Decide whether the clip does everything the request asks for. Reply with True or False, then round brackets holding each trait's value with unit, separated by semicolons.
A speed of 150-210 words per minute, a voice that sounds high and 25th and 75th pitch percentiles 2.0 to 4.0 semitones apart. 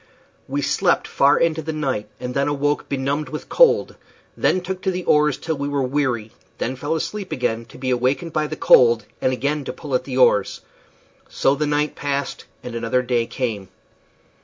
False (190 wpm; 140 Hz; 3.2 semitones)